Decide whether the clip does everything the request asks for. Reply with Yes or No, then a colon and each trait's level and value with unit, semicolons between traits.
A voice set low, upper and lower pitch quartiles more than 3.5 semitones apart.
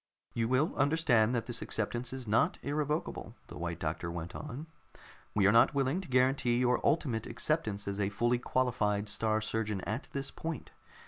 Yes: low, 120 Hz; average, 4.5 semitones